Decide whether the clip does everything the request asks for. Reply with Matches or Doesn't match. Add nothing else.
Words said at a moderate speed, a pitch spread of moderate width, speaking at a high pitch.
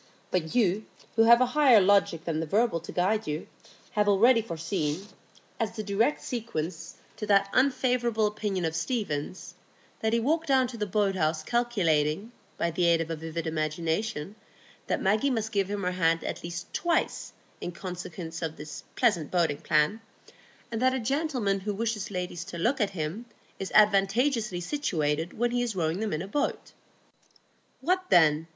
Doesn't match